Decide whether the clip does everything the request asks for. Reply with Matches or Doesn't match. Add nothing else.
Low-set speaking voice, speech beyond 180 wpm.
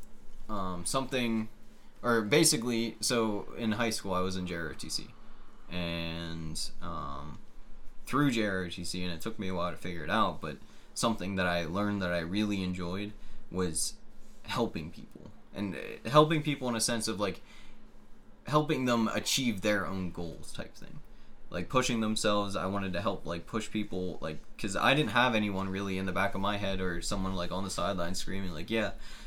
Doesn't match